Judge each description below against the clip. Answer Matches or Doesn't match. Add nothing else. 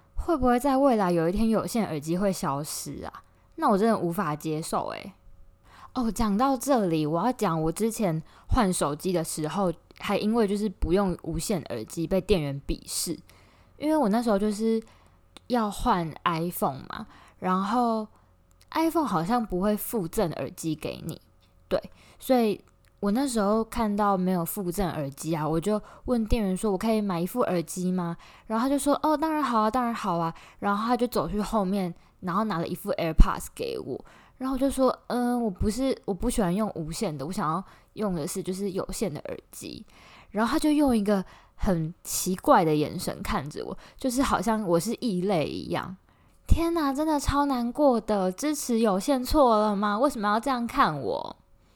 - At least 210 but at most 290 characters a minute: Matches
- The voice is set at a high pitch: Matches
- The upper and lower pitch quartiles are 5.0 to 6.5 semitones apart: Matches